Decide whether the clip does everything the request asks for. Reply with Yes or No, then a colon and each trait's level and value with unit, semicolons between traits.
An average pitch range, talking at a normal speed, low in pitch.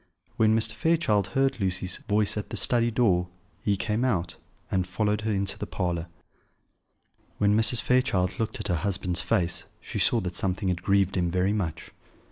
Yes: average, 3.4 semitones; average, 175 wpm; low, 100 Hz